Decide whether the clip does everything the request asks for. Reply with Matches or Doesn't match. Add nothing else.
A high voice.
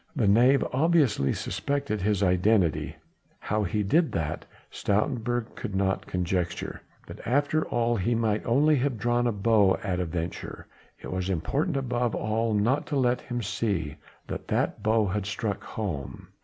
Doesn't match